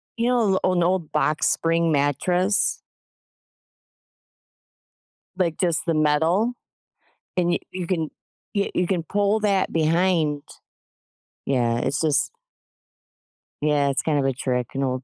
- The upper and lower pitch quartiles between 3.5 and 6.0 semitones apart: Yes, average, 4.3 semitones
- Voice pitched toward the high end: No, medium, 165 Hz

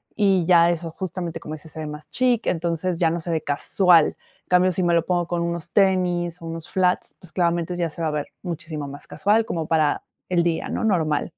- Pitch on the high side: No, medium, 170 Hz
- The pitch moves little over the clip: Yes, narrow, 2.0 semitones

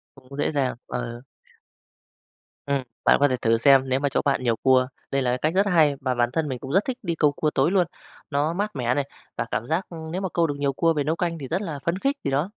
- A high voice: No, medium, 145 Hz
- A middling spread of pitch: Yes, average, 4.3 semitones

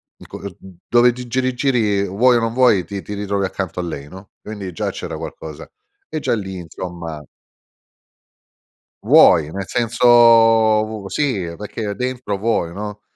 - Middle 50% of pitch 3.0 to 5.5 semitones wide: Yes, average, 4.4 semitones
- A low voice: Yes, low, 100 Hz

